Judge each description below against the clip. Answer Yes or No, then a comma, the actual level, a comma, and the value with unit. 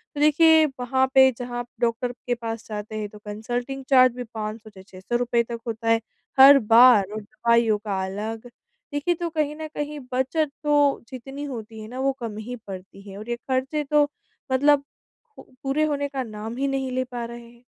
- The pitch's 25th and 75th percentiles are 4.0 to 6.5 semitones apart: No, average, 3.6 semitones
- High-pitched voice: Yes, high, 245 Hz